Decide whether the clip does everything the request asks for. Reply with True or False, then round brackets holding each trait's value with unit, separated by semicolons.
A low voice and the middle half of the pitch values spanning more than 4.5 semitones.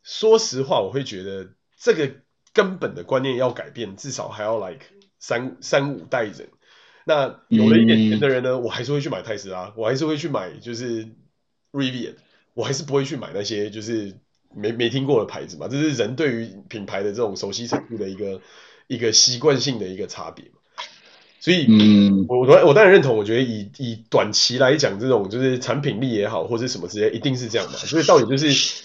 False (120 Hz; 4.1 semitones)